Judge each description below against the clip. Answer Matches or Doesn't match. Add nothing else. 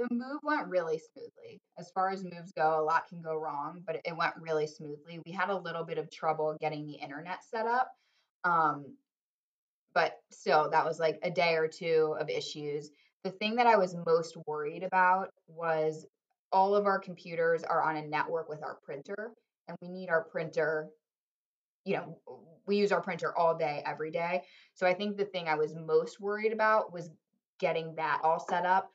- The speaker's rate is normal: Matches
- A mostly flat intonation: Doesn't match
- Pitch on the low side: Doesn't match